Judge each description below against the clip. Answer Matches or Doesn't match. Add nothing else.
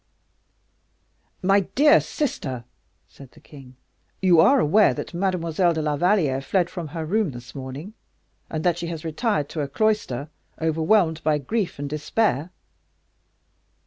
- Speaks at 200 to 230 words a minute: Doesn't match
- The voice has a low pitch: Doesn't match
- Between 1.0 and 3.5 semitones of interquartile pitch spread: Doesn't match